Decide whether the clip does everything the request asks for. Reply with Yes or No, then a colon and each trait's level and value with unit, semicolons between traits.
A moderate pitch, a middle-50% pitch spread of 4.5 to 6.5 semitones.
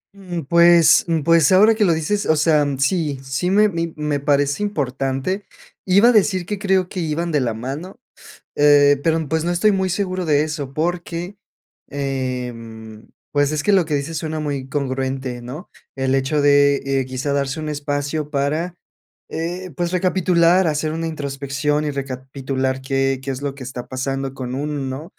No: medium, 150 Hz; average, 4.0 semitones